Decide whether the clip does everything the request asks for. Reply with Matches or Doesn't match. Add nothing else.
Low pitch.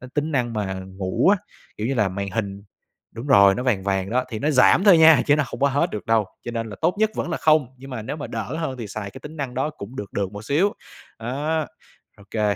Matches